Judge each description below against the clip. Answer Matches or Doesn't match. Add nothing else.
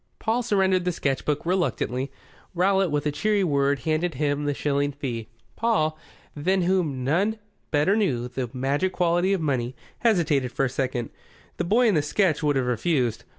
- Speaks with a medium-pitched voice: Matches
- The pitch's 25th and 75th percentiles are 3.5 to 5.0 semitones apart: Doesn't match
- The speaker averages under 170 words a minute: Doesn't match